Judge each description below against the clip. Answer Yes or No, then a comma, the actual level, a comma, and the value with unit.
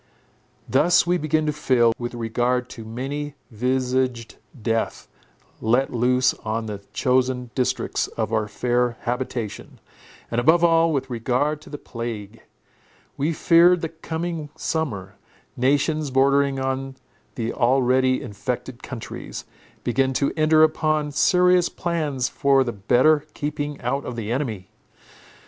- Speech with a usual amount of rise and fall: Yes, average, 3.9 semitones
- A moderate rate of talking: No, slow, 130 wpm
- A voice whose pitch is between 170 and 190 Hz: No, low, 130 Hz